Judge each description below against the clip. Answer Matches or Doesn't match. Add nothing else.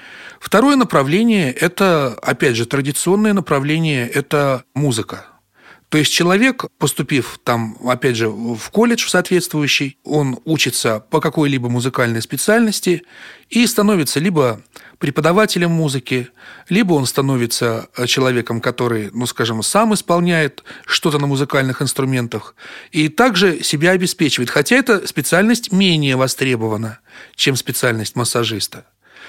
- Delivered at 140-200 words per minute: Doesn't match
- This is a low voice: Doesn't match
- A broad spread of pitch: Matches